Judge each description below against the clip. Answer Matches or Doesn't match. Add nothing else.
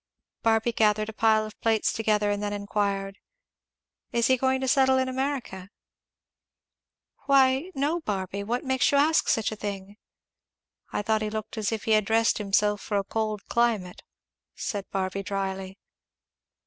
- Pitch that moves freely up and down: Doesn't match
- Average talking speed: Matches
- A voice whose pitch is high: Matches